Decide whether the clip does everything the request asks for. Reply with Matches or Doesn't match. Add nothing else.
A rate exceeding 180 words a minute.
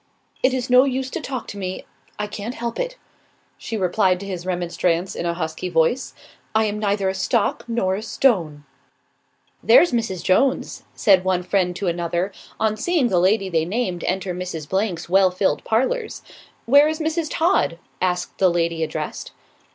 Doesn't match